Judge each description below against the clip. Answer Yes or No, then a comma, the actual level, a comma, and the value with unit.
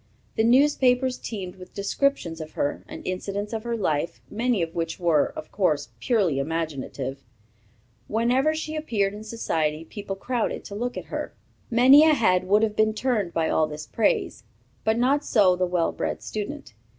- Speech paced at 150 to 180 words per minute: Yes, average, 170 wpm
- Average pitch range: No, wide, 6.4 semitones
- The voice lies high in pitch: Yes, high, 205 Hz